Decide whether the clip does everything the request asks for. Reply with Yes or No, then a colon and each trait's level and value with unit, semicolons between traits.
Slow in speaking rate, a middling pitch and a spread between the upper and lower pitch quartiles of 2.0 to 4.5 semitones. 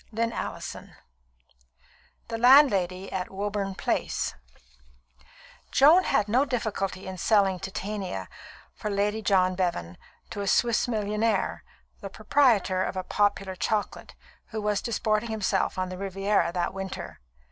No: slow, 125 wpm; high, 200 Hz; narrow, 2.6 semitones